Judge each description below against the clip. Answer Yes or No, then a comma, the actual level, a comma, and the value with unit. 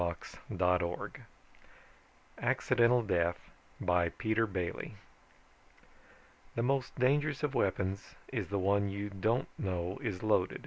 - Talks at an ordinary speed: No, slow, 105 wpm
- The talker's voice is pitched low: Yes, low, 100 Hz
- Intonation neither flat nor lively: Yes, average, 4.6 semitones